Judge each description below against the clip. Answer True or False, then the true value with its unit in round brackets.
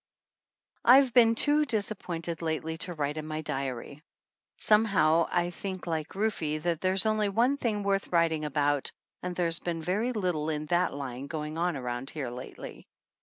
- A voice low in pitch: False (170 Hz)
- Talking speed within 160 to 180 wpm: True (165 wpm)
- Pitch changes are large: False (4.8 semitones)